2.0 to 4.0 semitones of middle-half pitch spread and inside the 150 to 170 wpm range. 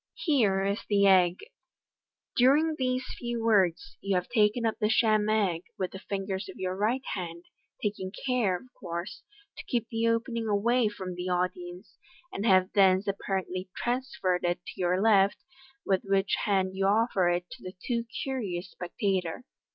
Yes: average, 3.7 semitones; average, 165 wpm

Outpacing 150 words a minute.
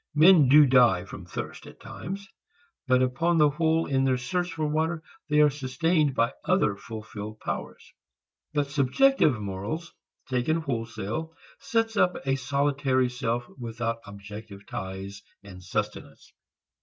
No: slow, 135 wpm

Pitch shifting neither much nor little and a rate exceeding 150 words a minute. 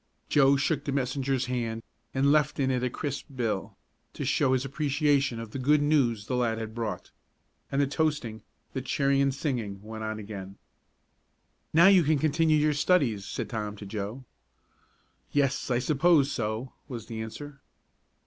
Yes: average, 4.3 semitones; average, 170 wpm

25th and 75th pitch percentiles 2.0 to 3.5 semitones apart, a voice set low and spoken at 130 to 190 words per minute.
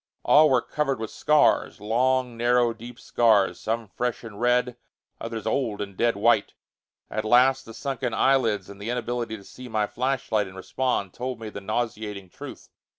Yes: average, 2.7 semitones; low, 115 Hz; average, 170 wpm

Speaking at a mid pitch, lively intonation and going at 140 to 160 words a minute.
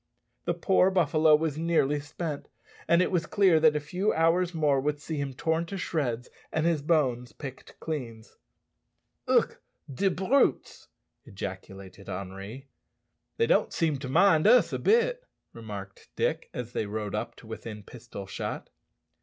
Yes: medium, 150 Hz; wide, 6.4 semitones; average, 155 wpm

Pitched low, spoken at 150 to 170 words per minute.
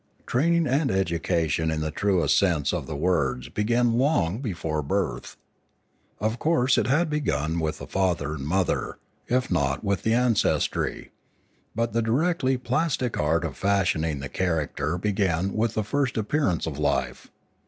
Yes: very low, 95 Hz; average, 155 wpm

